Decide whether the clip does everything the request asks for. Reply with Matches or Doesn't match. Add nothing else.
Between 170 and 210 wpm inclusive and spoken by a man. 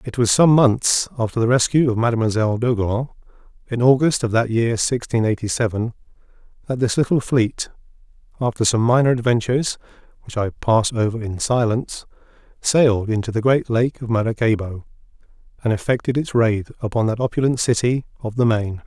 Doesn't match